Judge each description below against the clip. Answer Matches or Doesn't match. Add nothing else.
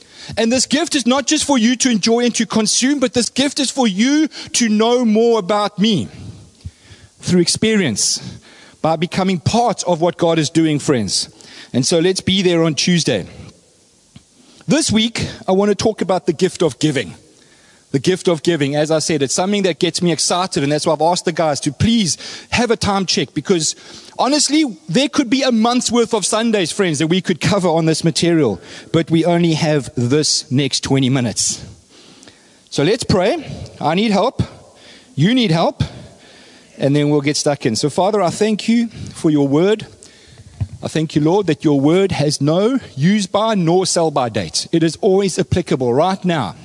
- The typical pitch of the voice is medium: Matches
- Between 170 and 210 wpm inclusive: Matches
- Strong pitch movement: Matches